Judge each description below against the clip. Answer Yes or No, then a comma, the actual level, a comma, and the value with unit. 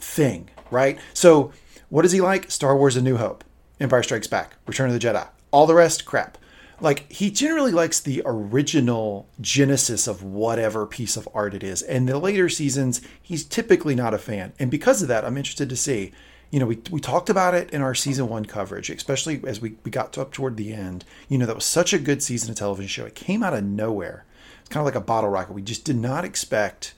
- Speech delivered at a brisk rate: Yes, fast, 230 wpm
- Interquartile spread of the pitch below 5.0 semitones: No, average, 5.3 semitones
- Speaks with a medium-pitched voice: No, low, 130 Hz